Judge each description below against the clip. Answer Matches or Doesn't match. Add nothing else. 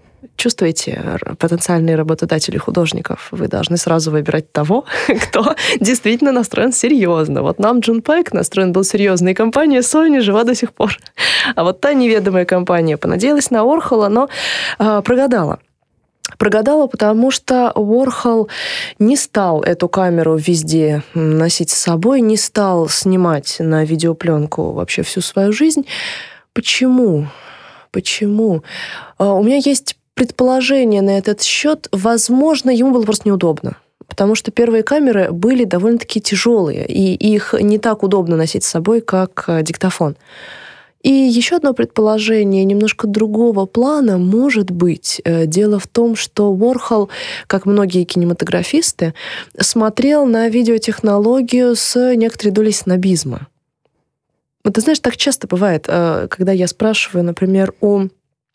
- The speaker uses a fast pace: Doesn't match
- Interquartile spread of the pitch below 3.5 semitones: Doesn't match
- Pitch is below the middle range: Doesn't match